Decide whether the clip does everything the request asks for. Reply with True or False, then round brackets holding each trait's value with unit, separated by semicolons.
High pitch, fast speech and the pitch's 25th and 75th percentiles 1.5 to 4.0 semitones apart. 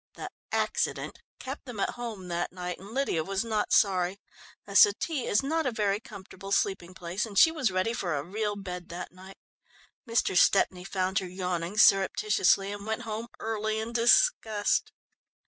False (200 Hz; 170 wpm; 3.4 semitones)